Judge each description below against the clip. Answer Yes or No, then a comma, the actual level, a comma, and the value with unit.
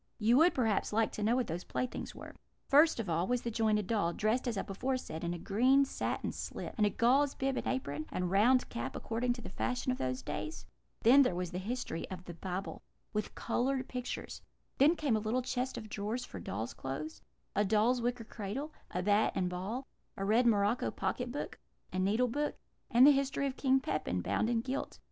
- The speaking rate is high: Yes, fast, 215 wpm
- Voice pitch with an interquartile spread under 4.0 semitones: No, average, 4.8 semitones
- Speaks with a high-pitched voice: Yes, high, 225 Hz